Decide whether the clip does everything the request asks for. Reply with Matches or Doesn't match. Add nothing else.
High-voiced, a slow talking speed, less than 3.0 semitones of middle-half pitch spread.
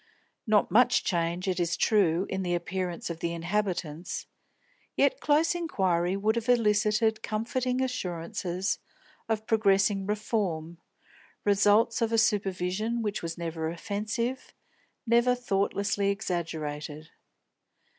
Doesn't match